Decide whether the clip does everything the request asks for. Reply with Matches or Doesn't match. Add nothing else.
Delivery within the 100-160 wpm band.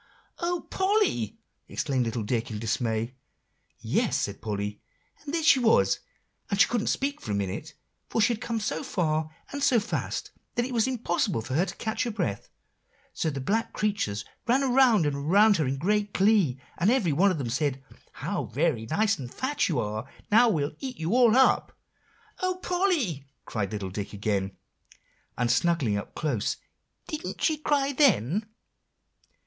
Doesn't match